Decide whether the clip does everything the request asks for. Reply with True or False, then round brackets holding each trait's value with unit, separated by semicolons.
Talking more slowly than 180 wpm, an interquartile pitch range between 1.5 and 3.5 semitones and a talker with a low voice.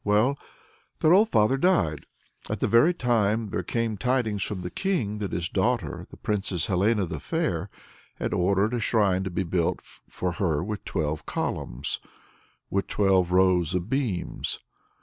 False (160 wpm; 4.5 semitones; 100 Hz)